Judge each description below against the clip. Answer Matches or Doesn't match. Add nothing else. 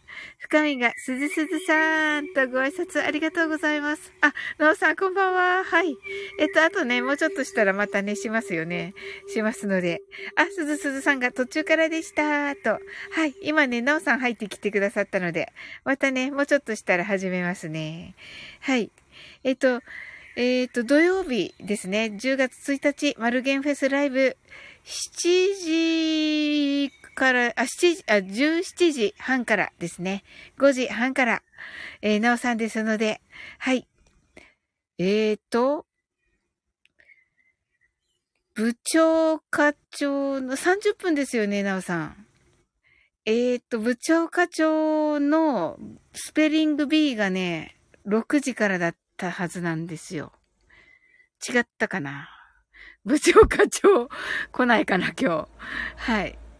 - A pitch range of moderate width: Doesn't match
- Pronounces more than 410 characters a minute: Doesn't match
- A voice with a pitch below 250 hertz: Doesn't match